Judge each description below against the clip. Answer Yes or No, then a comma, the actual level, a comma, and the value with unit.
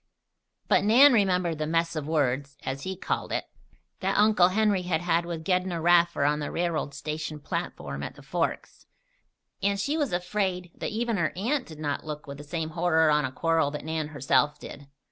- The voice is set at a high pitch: No, medium, 165 Hz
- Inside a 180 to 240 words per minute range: Yes, average, 195 wpm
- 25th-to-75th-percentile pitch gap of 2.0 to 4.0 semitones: Yes, average, 3.7 semitones